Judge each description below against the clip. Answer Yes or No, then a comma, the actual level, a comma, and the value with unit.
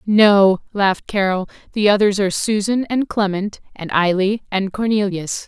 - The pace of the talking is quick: No, average, 140 wpm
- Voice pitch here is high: Yes, high, 200 Hz